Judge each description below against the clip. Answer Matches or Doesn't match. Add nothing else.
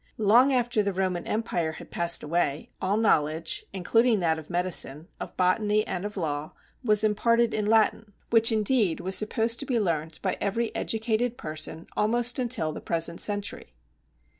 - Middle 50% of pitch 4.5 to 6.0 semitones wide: Matches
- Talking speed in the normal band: Matches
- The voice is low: Doesn't match